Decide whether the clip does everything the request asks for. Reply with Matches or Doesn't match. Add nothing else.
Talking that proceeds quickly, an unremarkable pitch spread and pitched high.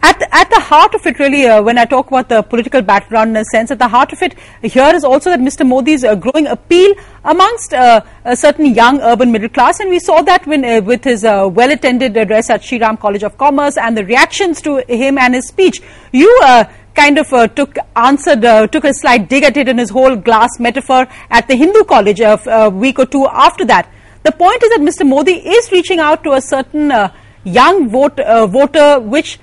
Matches